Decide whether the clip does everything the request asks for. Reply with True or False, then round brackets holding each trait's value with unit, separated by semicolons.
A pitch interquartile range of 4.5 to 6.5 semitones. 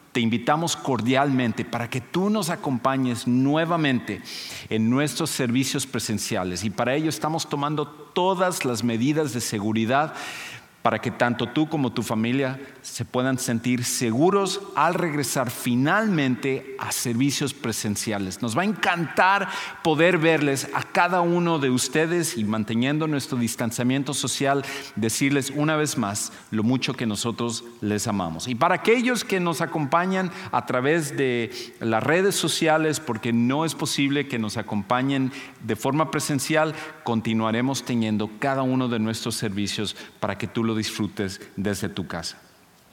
True (5.0 semitones)